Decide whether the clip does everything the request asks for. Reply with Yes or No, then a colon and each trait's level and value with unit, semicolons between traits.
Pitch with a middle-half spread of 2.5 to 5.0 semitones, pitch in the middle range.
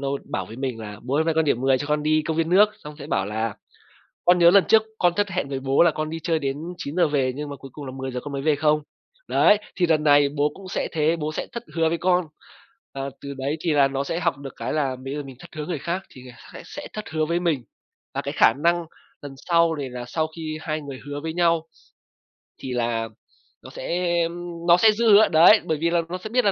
Yes: average, 3.8 semitones; medium, 155 Hz